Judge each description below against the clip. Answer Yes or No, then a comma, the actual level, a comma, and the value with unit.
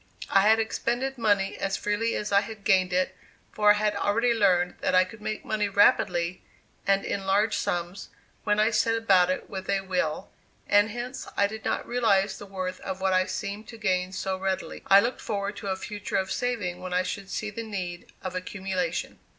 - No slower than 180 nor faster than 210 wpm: Yes, fast, 205 wpm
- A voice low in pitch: No, high, 200 Hz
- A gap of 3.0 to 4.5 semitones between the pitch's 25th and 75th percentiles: No, narrow, 2.4 semitones